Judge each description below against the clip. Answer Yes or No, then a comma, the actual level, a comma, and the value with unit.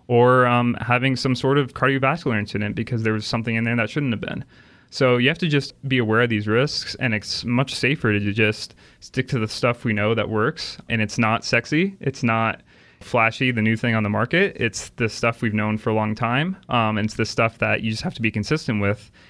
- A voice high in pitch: No, low, 115 Hz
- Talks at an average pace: No, fast, 240 wpm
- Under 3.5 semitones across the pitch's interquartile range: Yes, average, 3.0 semitones